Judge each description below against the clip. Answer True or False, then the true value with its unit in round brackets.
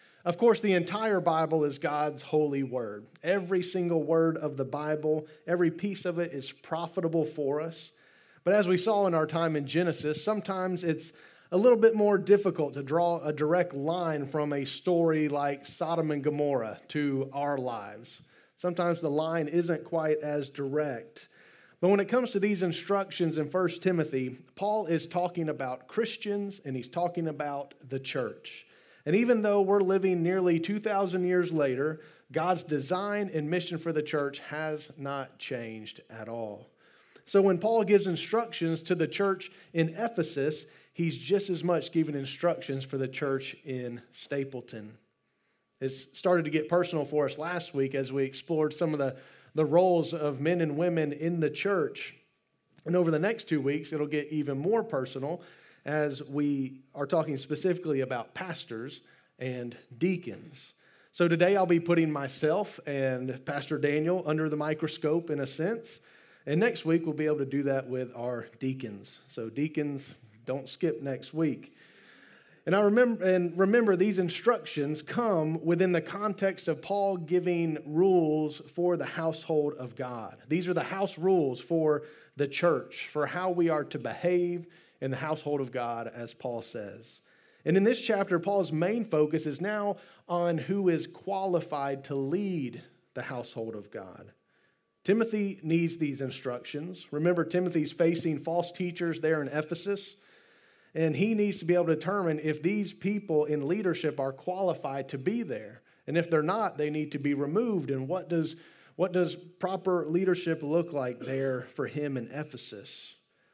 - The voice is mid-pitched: True (160 Hz)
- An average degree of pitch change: True (4.0 semitones)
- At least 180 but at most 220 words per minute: False (165 wpm)